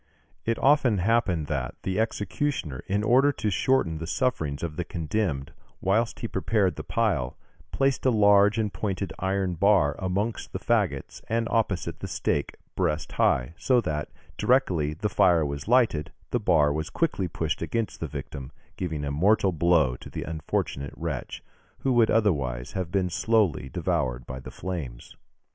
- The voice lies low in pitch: Yes, very low, 90 Hz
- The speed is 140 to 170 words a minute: Yes, average, 160 wpm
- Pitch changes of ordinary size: No, wide, 6.5 semitones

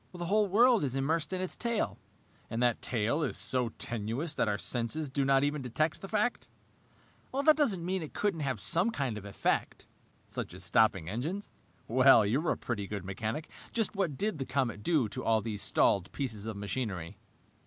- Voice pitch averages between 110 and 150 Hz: Yes, low, 135 Hz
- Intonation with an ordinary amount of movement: No, wide, 7.8 semitones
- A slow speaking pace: No, average, 190 wpm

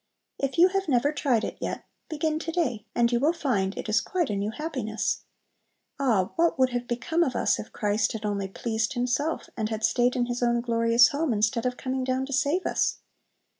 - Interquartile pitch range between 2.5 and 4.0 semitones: No, average, 4.4 semitones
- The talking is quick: Yes, fast, 210 wpm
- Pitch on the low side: No, high, 245 Hz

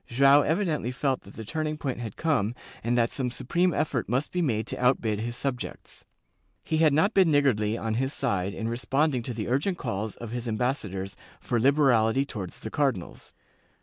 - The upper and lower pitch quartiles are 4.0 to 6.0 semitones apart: Yes, average, 4.4 semitones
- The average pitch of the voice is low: Yes, low, 125 Hz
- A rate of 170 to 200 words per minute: Yes, average, 185 wpm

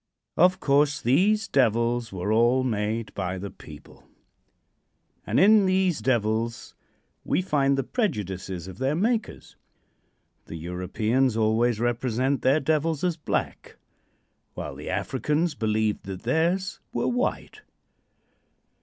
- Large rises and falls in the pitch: Yes, wide, 6.9 semitones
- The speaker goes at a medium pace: No, slow, 120 wpm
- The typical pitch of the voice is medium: No, low, 130 Hz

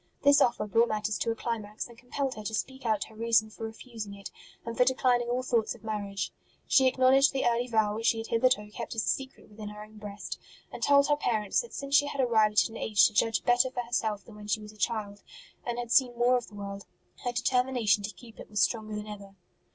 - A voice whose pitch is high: Yes, high, 225 Hz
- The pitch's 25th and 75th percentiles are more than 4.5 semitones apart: No, average, 2.9 semitones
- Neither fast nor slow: No, fast, 245 wpm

